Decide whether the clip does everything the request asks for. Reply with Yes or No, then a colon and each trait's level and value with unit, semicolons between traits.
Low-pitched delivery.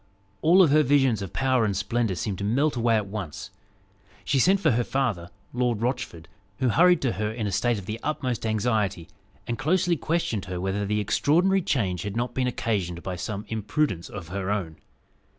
Yes: low, 110 Hz